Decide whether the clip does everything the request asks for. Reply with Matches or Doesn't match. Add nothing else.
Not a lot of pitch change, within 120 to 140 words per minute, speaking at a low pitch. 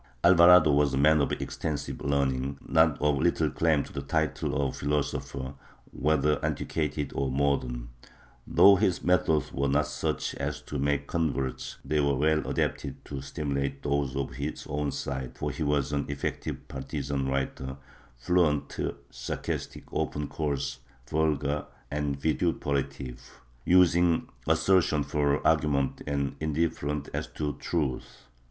Matches